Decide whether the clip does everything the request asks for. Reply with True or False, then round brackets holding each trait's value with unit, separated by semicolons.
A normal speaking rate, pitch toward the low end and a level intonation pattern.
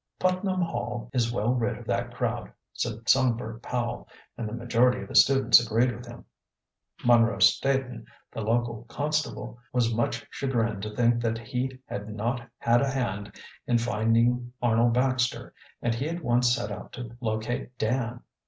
True (160 wpm; 120 Hz; 1.6 semitones)